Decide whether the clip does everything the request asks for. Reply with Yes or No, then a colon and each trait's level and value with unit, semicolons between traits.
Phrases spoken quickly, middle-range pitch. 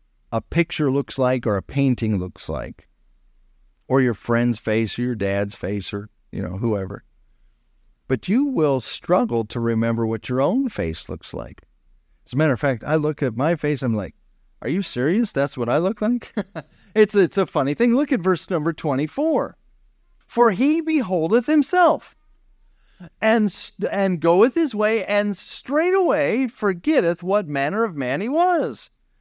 No: average, 170 wpm; medium, 150 Hz